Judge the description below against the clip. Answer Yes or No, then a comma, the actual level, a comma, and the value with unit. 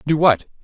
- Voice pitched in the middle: Yes, medium, 145 Hz